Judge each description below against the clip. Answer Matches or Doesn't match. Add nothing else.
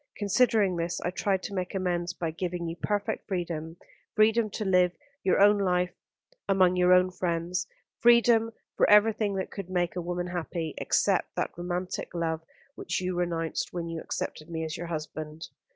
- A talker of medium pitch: Matches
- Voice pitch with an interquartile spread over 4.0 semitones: Doesn't match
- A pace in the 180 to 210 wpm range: Doesn't match